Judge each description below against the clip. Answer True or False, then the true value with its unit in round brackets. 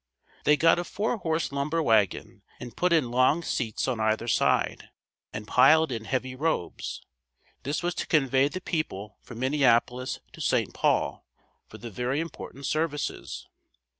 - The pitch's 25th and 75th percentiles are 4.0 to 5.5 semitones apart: True (5.0 semitones)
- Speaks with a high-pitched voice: False (135 Hz)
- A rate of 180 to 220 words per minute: False (155 wpm)